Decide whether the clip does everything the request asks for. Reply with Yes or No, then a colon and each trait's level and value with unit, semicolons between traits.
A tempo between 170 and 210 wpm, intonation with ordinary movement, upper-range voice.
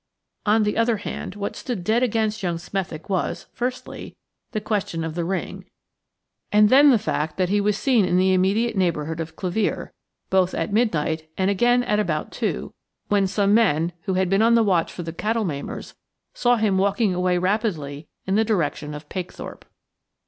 Yes: average, 185 wpm; average, 3.9 semitones; high, 195 Hz